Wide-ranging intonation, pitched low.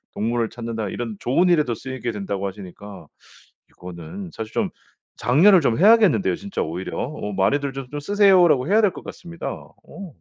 Yes: wide, 9.0 semitones; low, 125 Hz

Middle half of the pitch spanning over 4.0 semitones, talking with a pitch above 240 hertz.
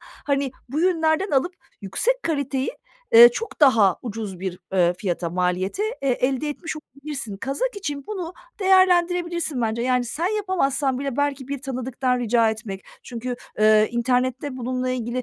Yes: average, 5.0 semitones; very high, 260 Hz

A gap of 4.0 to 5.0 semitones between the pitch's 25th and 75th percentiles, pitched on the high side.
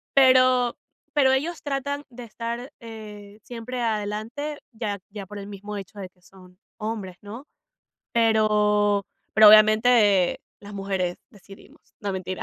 No: average, 3.3 semitones; high, 215 Hz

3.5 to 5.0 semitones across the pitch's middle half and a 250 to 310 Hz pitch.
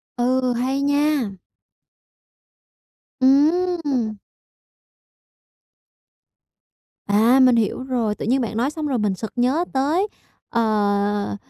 Yes: average, 4.4 semitones; very high, 255 Hz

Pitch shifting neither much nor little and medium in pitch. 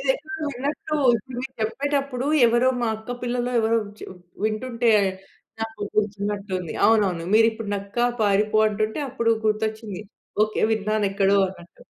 No: average, 3.0 semitones; high, 220 Hz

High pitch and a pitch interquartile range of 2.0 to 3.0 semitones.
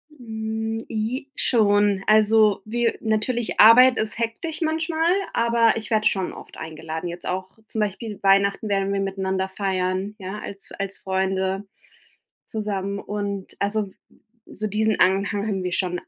Yes: high, 205 Hz; narrow, 2.5 semitones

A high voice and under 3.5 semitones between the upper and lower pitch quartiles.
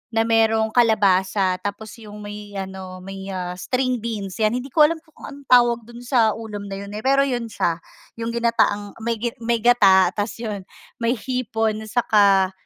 Yes: high, 220 Hz; average, 2.9 semitones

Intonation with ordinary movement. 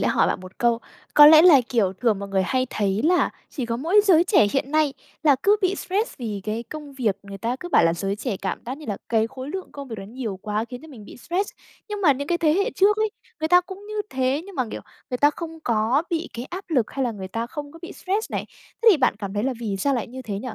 No: wide, 7.1 semitones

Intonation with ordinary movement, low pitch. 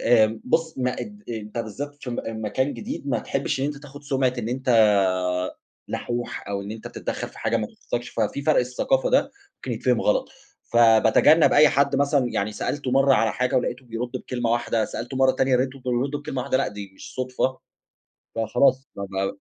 Yes: average, 3.3 semitones; low, 125 Hz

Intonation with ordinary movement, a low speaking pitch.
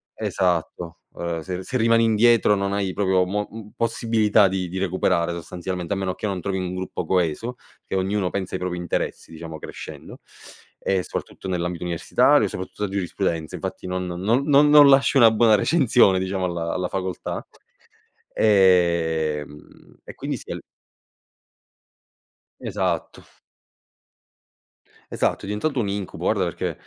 Yes: average, 3.0 semitones; very low, 95 Hz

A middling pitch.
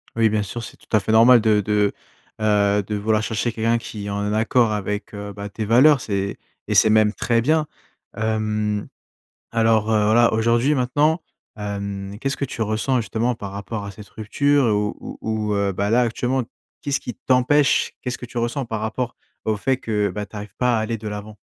No: low, 110 Hz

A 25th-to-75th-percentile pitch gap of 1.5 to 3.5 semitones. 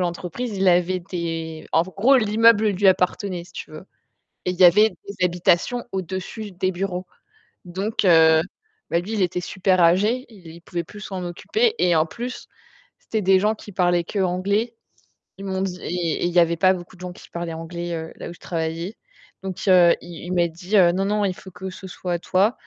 Yes: narrow, 2.5 semitones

